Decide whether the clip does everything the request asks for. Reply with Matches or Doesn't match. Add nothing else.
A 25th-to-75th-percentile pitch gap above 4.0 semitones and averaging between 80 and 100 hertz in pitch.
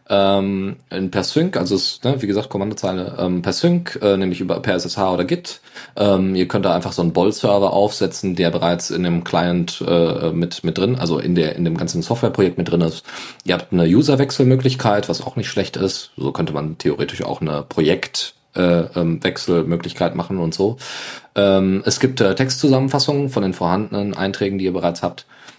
Doesn't match